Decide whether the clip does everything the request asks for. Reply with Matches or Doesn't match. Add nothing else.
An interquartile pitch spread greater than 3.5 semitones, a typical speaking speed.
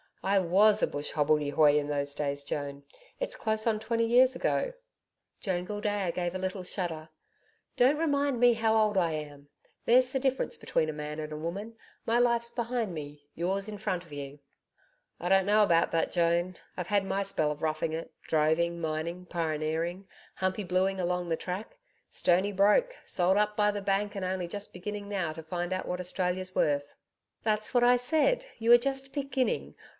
Matches